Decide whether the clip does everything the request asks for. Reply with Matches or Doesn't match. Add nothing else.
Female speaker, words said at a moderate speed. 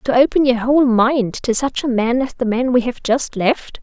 Doesn't match